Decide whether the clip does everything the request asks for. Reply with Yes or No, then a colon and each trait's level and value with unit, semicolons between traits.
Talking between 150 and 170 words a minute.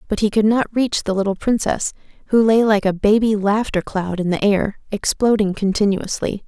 No: average, 185 wpm